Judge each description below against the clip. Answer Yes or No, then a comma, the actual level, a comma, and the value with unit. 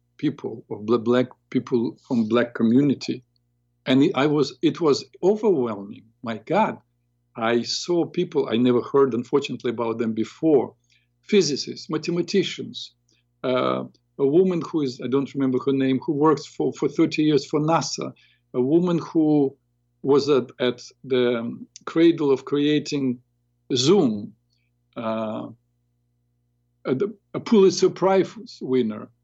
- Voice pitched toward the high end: No, low, 125 Hz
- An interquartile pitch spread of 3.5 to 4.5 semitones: Yes, average, 3.8 semitones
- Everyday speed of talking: No, slow, 125 wpm